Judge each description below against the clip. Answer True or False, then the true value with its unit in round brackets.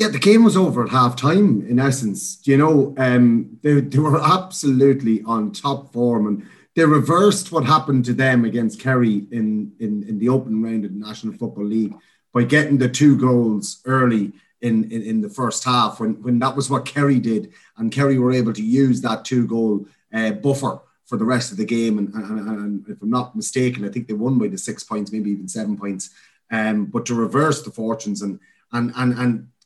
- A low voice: True (120 Hz)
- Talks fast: True (210 wpm)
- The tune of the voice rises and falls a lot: False (4.0 semitones)